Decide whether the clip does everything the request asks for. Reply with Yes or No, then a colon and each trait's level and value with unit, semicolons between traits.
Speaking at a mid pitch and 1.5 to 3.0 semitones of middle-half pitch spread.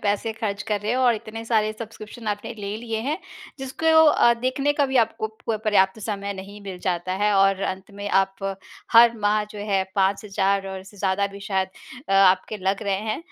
No: high, 205 Hz; narrow, 2.5 semitones